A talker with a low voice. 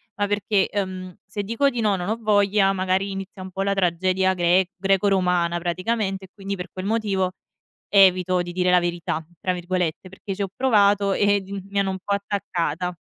No: high, 190 Hz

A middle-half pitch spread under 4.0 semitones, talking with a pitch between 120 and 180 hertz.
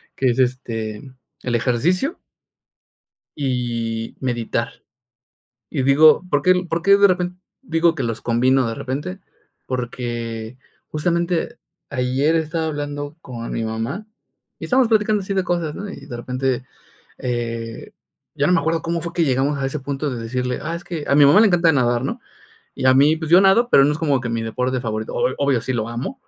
No: wide, 5.5 semitones; medium, 140 Hz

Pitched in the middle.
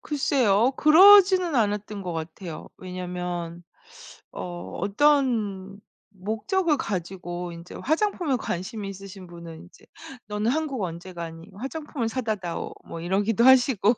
No: high, 205 Hz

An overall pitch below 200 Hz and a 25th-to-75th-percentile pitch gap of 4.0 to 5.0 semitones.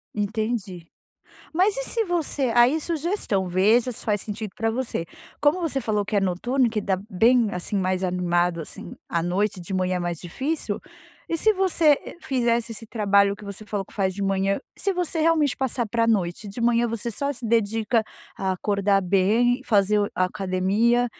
No: high, 215 Hz; average, 4.5 semitones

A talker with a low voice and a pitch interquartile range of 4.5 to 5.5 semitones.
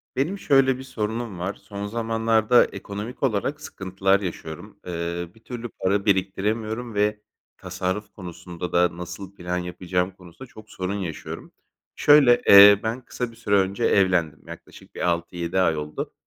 No: low, 100 Hz; average, 4.1 semitones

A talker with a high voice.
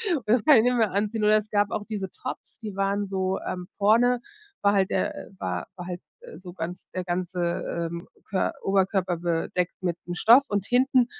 Yes: high, 195 Hz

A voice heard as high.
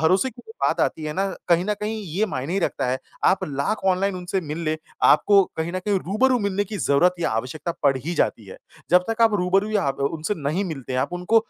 No: medium, 180 Hz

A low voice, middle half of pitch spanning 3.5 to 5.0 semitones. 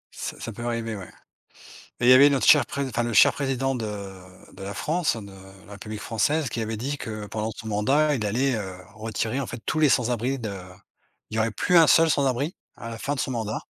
Yes: low, 120 Hz; average, 4.2 semitones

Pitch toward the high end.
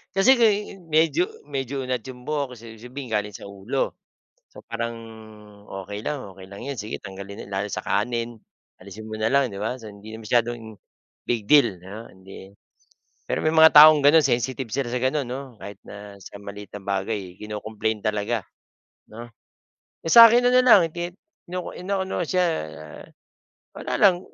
No: low, 115 Hz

